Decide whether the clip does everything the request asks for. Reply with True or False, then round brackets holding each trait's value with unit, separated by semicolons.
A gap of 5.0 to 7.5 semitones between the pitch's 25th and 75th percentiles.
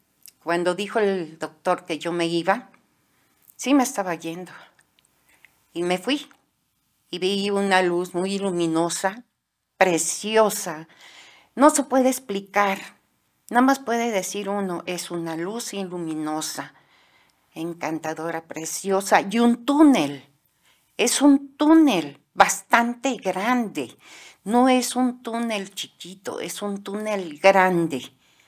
True (5.6 semitones)